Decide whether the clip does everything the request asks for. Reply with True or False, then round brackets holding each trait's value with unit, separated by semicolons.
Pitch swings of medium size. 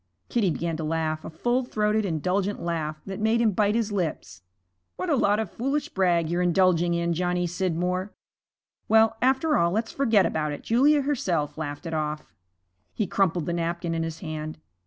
True (5.0 semitones)